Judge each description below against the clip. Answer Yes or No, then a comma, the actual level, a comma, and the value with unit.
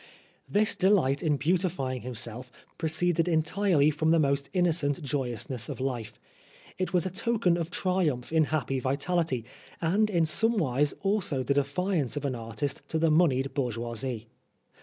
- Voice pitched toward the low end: No, medium, 150 Hz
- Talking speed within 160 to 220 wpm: No, average, 145 wpm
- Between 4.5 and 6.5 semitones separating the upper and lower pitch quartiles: Yes, average, 5.1 semitones